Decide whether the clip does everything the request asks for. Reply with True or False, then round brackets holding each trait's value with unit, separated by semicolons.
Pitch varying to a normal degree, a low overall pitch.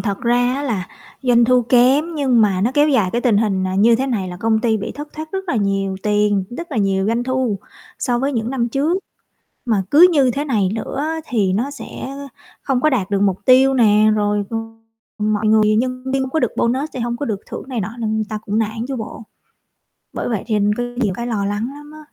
False (4.1 semitones; 235 Hz)